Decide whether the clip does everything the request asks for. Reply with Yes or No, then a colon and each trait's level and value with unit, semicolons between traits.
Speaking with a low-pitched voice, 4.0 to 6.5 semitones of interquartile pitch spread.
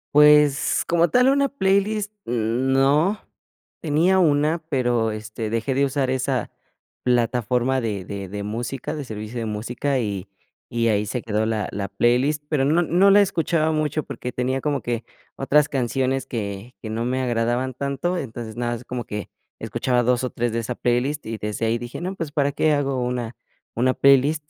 Yes: low, 130 Hz; average, 4.4 semitones